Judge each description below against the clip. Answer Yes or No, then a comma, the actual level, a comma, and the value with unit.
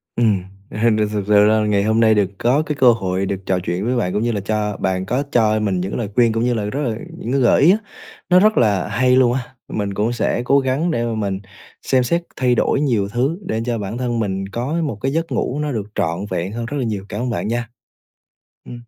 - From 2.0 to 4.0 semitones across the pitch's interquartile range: Yes, average, 3.7 semitones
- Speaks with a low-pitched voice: Yes, low, 115 Hz